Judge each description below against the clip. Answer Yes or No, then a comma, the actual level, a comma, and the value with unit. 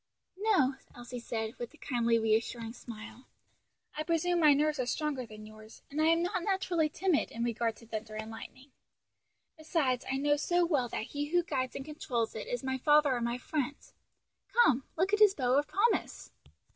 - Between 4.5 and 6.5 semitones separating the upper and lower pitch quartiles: Yes, average, 5.1 semitones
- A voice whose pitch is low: No, very high, 270 Hz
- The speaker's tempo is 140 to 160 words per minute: No, average, 190 wpm